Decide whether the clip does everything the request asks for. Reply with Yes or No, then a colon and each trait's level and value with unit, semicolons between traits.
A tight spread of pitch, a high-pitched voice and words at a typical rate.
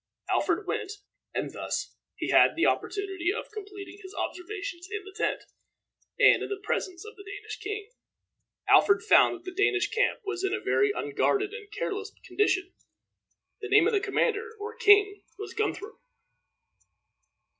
Yes: narrow, 1.5 semitones; very high, 405 Hz; average, 155 wpm